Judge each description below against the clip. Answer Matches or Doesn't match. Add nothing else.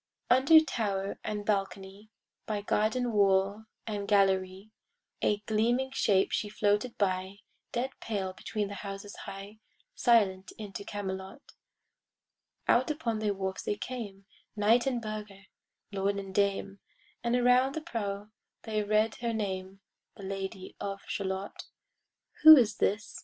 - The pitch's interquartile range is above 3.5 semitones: Doesn't match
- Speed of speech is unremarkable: Doesn't match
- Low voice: Doesn't match